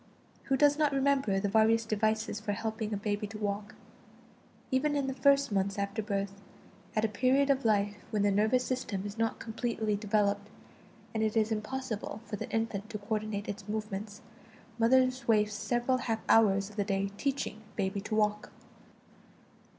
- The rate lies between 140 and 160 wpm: No, average, 170 wpm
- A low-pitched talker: No, high, 215 Hz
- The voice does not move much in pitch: Yes, narrow, 2.3 semitones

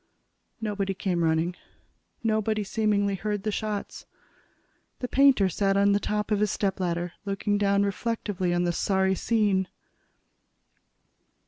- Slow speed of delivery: Yes, slow, 125 wpm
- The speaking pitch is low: No, high, 200 Hz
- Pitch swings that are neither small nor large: No, narrow, 1.9 semitones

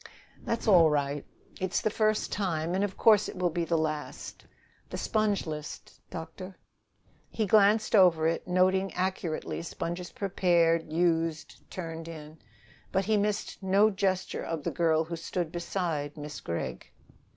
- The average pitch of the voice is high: No, medium, 175 Hz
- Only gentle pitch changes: No, average, 3.2 semitones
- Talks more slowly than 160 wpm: Yes, average, 150 wpm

